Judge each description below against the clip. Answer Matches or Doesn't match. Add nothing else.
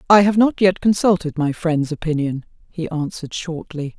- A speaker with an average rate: Matches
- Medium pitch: Matches